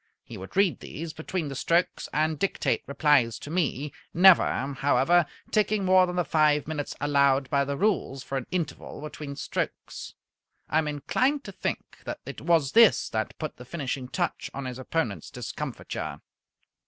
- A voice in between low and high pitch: Yes, medium, 150 Hz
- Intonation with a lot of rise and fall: No, average, 4.1 semitones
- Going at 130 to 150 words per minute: No, average, 165 wpm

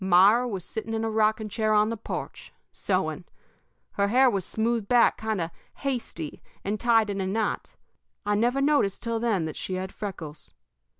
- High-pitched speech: Yes, high, 215 Hz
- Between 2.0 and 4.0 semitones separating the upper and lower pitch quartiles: Yes, average, 2.8 semitones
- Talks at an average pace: Yes, average, 180 wpm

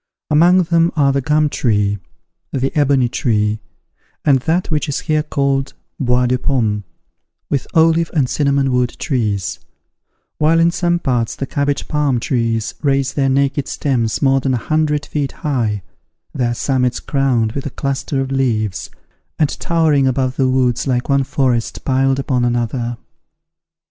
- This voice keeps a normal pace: Yes, average, 155 wpm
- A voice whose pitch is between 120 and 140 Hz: Yes, low, 135 Hz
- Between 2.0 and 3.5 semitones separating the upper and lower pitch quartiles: Yes, average, 3.1 semitones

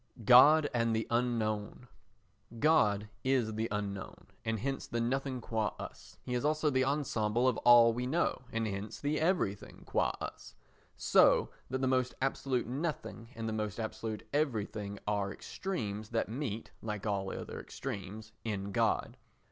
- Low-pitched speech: Yes, low, 115 Hz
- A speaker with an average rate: Yes, average, 155 wpm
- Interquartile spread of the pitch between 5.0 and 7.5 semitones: No, average, 3.6 semitones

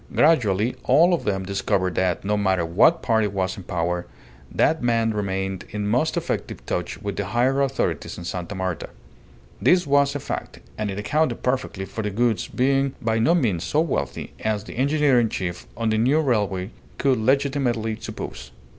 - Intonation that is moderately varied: No, wide, 5.8 semitones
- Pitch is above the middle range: No, low, 110 Hz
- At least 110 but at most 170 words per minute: No, average, 180 wpm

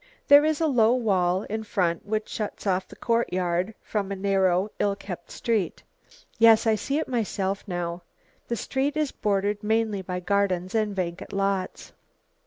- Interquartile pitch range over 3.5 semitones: No, average, 3.2 semitones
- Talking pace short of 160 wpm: No, average, 165 wpm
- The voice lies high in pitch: Yes, high, 200 Hz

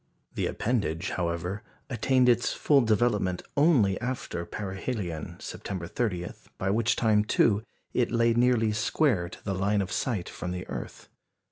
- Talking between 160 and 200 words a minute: No, average, 145 wpm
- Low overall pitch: Yes, low, 105 Hz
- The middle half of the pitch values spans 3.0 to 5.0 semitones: Yes, average, 4.6 semitones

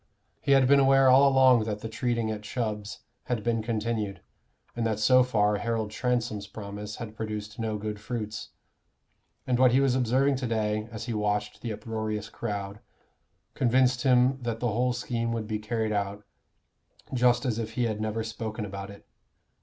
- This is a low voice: Yes, low, 115 Hz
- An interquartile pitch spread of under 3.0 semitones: Yes, narrow, 2.6 semitones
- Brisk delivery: No, average, 175 wpm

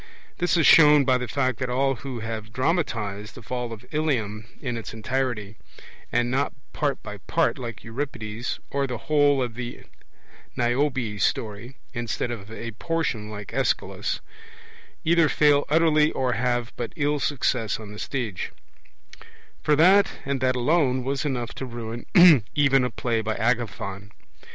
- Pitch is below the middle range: Yes, low, 125 Hz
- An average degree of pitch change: Yes, average, 4.0 semitones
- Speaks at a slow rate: No, average, 150 wpm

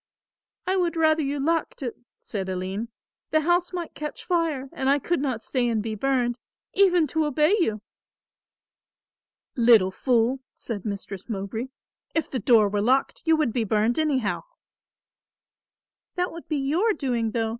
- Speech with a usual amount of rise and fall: No, wide, 6.0 semitones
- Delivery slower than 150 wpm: No, average, 155 wpm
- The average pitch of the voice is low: No, very high, 265 Hz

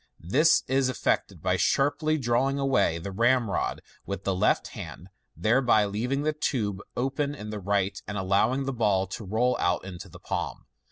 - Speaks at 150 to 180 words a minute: Yes, average, 170 wpm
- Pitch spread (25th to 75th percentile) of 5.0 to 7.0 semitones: Yes, wide, 5.5 semitones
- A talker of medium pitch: No, low, 115 Hz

